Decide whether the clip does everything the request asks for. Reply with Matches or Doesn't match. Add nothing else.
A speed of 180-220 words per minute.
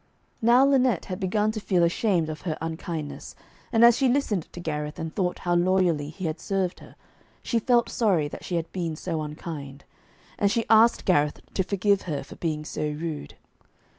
Matches